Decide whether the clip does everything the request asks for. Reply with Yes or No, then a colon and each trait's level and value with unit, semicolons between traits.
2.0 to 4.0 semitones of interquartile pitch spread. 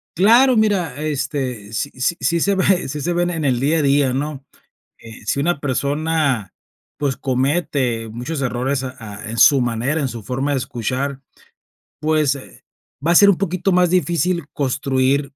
No: average, 4.4 semitones